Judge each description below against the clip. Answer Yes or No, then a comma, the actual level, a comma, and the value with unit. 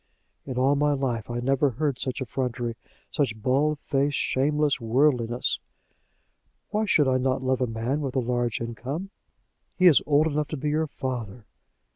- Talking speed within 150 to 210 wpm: Yes, average, 160 wpm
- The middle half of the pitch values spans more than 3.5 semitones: No, average, 3.2 semitones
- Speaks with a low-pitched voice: Yes, low, 130 Hz